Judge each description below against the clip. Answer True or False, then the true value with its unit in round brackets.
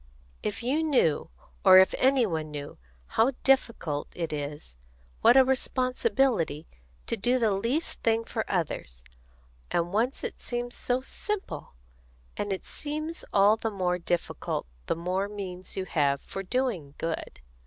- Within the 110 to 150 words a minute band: True (145 wpm)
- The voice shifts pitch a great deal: True (7.1 semitones)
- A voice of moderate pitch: False (205 Hz)